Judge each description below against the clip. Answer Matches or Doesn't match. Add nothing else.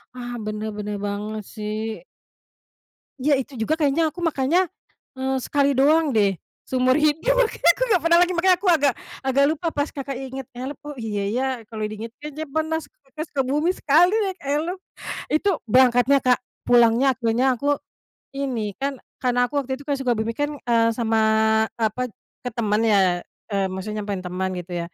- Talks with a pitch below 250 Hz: Doesn't match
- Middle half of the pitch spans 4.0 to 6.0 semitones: Matches